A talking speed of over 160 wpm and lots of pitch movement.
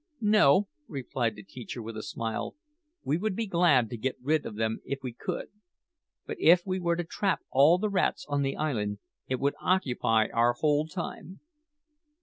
Yes: average, 180 wpm; wide, 6.6 semitones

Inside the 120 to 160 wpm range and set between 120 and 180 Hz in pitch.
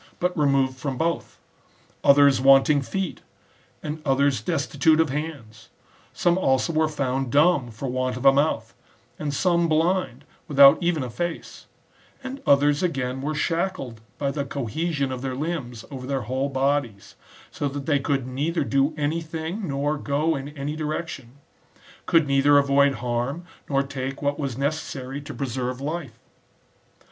Yes: average, 155 wpm; medium, 140 Hz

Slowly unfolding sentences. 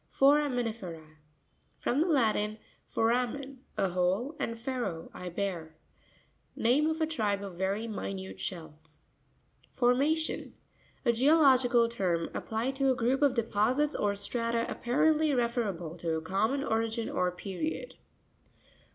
Yes: slow, 125 wpm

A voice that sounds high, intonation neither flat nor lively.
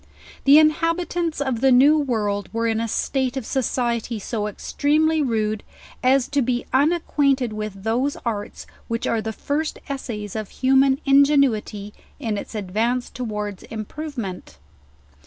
Yes: high, 245 Hz; average, 4.5 semitones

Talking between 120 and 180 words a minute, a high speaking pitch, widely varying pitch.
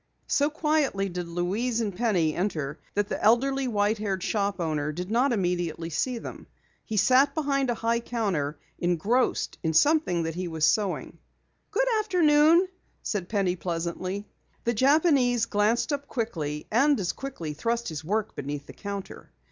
Yes: average, 155 wpm; high, 205 Hz; wide, 6.5 semitones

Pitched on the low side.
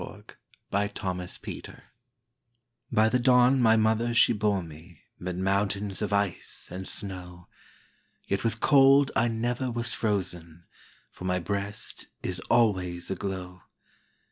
Yes: low, 100 Hz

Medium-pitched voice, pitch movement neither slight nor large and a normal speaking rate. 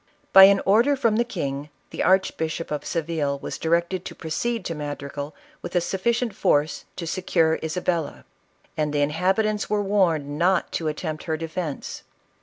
Yes: medium, 170 Hz; average, 4.1 semitones; average, 170 wpm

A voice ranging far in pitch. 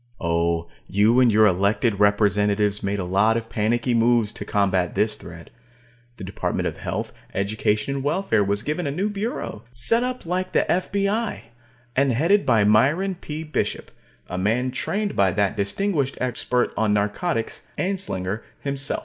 Yes: wide, 6.9 semitones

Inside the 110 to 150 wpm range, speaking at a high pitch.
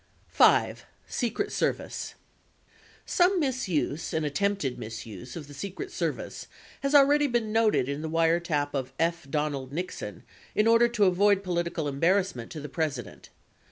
No: average, 145 wpm; medium, 170 Hz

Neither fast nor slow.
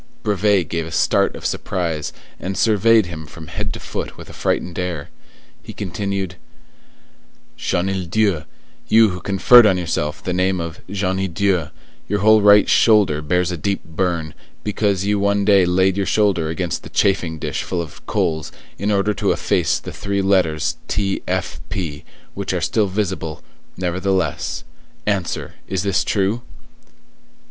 Yes: average, 155 wpm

